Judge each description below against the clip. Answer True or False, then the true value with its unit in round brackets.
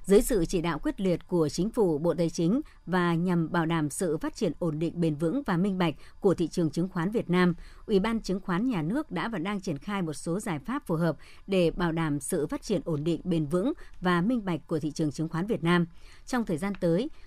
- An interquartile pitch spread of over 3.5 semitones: False (3.2 semitones)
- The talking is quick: True (255 wpm)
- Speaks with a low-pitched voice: False (175 Hz)